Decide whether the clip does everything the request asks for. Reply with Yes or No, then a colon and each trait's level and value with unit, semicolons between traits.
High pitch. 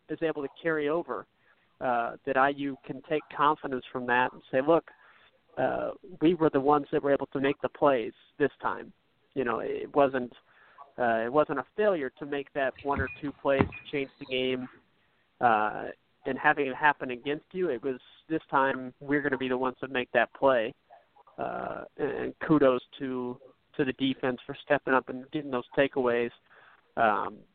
No: medium, 140 Hz